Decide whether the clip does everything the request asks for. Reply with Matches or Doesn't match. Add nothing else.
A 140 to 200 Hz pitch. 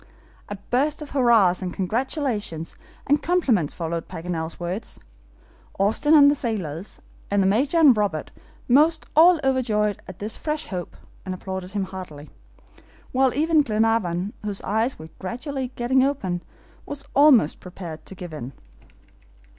Doesn't match